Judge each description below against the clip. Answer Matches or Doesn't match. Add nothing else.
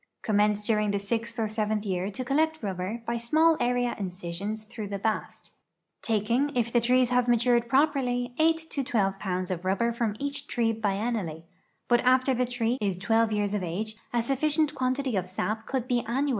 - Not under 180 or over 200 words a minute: Matches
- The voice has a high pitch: Matches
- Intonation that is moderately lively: Matches